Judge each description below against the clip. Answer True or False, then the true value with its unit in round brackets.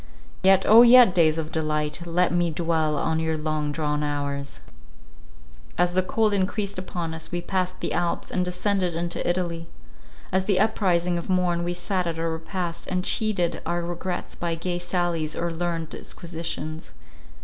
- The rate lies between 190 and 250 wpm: False (165 wpm)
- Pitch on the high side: False (175 Hz)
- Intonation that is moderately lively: False (2.1 semitones)